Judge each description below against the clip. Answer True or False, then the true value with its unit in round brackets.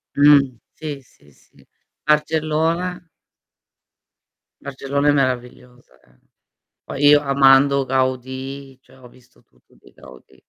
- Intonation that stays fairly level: True (2.3 semitones)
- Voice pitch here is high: False (135 Hz)